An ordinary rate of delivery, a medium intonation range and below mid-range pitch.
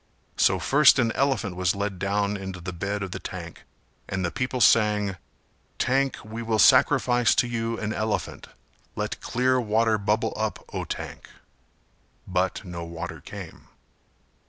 Yes: average, 150 wpm; average, 3.2 semitones; low, 105 Hz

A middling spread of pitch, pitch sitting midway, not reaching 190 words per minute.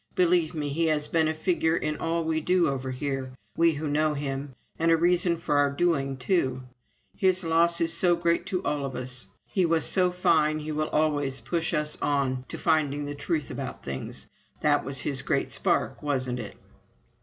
No: average, 3.2 semitones; medium, 155 Hz; average, 195 wpm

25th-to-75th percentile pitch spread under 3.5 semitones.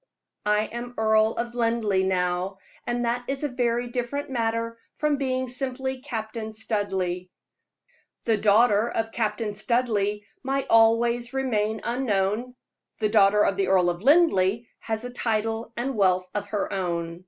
Yes: average, 3.1 semitones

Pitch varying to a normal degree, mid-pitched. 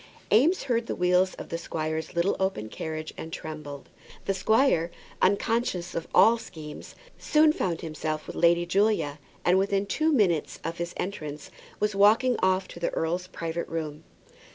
Yes: average, 4.1 semitones; medium, 175 Hz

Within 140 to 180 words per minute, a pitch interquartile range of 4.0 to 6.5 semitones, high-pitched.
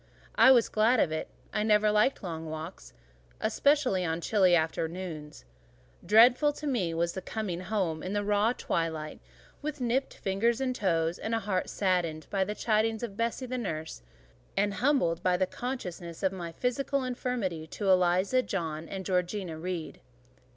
Yes: average, 165 wpm; wide, 5.4 semitones; high, 195 Hz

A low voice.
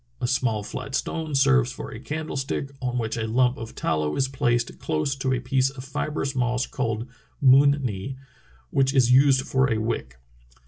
Yes: low, 130 Hz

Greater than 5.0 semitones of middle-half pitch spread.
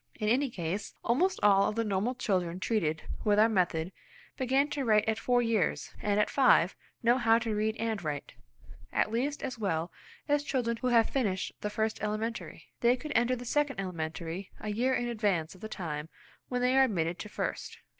No: average, 4.4 semitones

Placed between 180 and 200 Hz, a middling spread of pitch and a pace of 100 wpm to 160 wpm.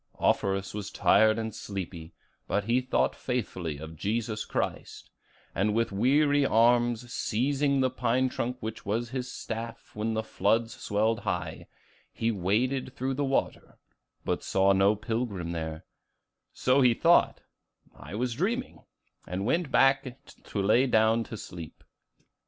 No: low, 115 Hz; average, 4.0 semitones; average, 140 wpm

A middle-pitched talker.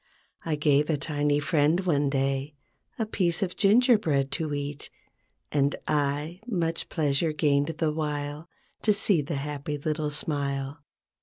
Yes: medium, 150 Hz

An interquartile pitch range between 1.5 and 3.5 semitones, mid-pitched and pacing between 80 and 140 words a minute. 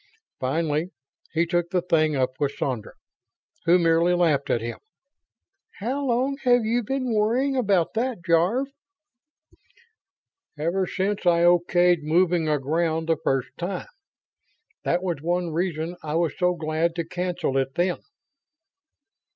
Yes: average, 3.0 semitones; medium, 175 Hz; slow, 135 wpm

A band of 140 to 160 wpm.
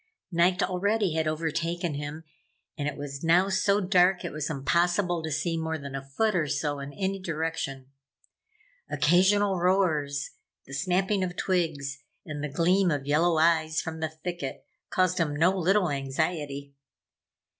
Yes: average, 155 wpm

